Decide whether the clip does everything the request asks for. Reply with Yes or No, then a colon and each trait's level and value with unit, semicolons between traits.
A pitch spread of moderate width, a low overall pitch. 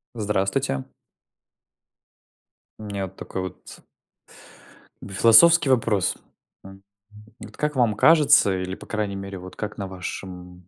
Yes: average, 3.2 semitones; low, 100 Hz